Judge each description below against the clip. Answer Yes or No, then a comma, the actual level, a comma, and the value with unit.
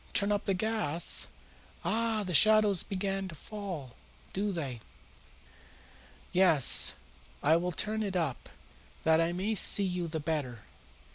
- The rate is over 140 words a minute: No, slow, 135 wpm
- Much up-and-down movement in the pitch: No, average, 4.3 semitones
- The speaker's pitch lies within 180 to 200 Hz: Yes, medium, 185 Hz